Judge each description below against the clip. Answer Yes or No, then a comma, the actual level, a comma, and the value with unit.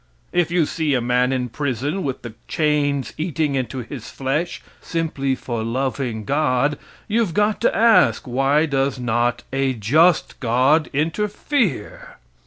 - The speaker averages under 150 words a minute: Yes, average, 140 wpm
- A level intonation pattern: No, average, 4.2 semitones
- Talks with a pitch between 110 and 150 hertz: Yes, medium, 140 Hz